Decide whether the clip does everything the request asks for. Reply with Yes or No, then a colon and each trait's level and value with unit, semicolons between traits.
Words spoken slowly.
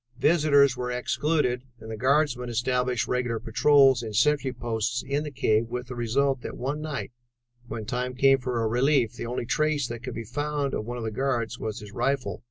No: average, 200 wpm